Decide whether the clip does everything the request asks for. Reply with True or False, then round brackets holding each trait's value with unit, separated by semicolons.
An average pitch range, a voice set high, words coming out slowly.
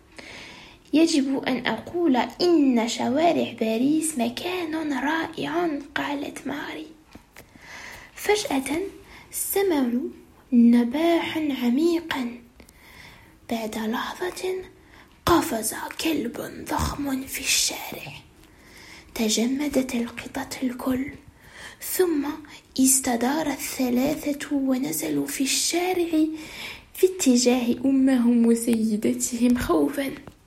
True (4.3 semitones; 280 Hz; 70 wpm)